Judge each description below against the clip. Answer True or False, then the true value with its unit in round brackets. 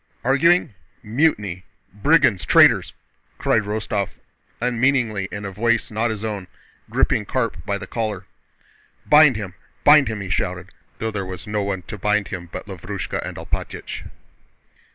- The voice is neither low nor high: False (105 Hz)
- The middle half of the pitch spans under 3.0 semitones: False (3.3 semitones)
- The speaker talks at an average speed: True (145 wpm)